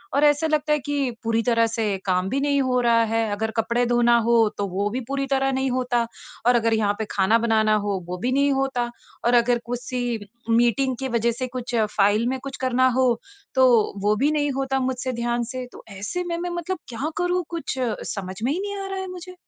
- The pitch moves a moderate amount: Yes, average, 3.3 semitones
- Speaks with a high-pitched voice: Yes, very high, 250 Hz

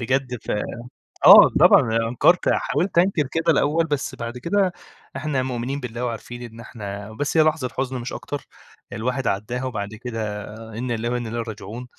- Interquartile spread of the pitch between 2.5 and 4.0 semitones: Yes, average, 3.7 semitones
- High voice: No, low, 125 Hz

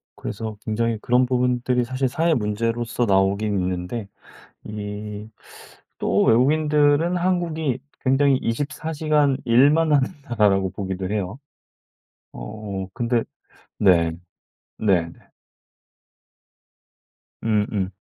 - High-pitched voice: No, low, 115 Hz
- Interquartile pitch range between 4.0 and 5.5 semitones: Yes, average, 5.2 semitones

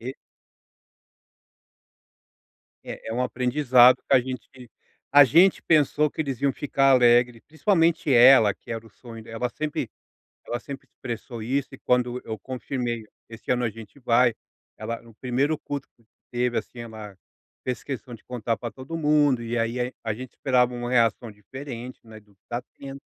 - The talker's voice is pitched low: Yes, low, 125 Hz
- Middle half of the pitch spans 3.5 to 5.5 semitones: No, narrow, 2.6 semitones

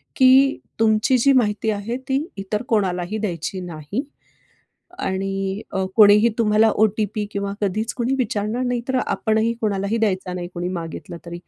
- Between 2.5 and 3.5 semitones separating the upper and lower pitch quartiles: Yes, average, 2.9 semitones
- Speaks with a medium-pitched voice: No, high, 210 Hz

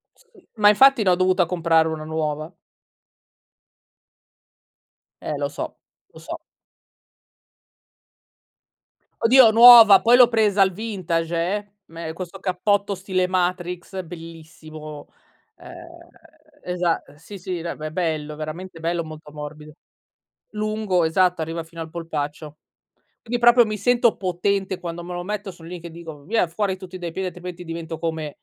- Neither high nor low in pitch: Yes, medium, 180 Hz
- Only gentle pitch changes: No, average, 3.7 semitones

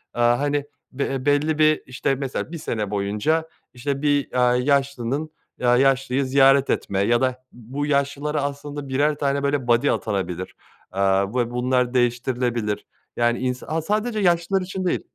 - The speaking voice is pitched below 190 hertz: Yes, low, 135 Hz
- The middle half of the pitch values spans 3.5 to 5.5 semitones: No, average, 3.1 semitones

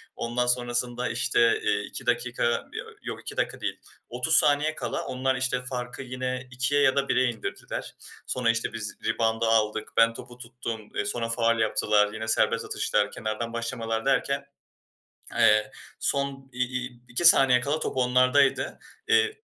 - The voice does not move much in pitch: Yes, narrow, 2.1 semitones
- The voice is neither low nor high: No, low, 125 Hz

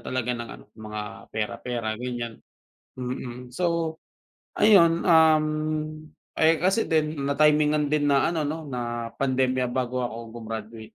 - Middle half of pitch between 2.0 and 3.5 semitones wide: No, average, 4.7 semitones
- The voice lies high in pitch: No, low, 130 Hz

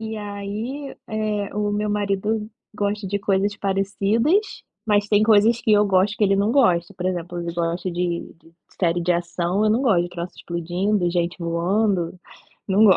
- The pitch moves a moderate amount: Yes, average, 3.2 semitones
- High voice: Yes, high, 200 Hz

